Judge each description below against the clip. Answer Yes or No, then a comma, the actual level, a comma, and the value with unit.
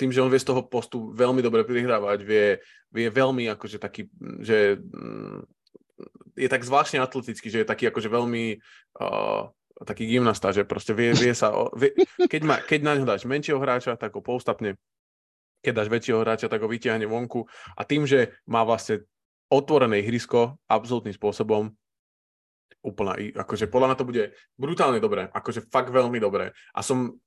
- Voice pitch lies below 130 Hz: Yes, low, 120 Hz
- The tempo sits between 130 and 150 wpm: No, fast, 165 wpm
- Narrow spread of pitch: No, average, 3.0 semitones